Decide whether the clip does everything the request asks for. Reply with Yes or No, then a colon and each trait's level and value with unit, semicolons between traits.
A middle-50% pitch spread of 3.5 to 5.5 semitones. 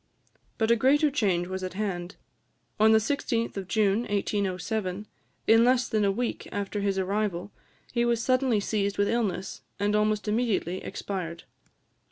No: average, 3.0 semitones